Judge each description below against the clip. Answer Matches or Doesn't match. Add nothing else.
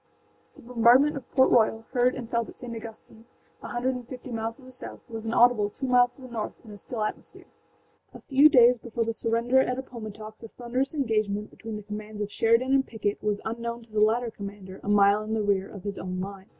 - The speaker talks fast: Matches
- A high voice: Matches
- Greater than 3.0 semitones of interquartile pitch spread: Doesn't match